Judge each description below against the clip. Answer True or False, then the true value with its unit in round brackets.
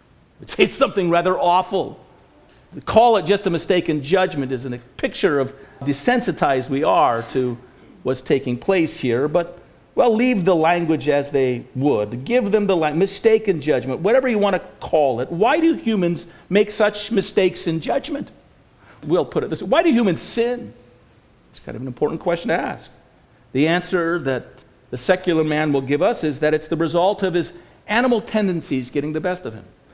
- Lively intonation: True (5.9 semitones)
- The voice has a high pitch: False (170 Hz)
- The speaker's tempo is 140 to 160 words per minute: False (190 wpm)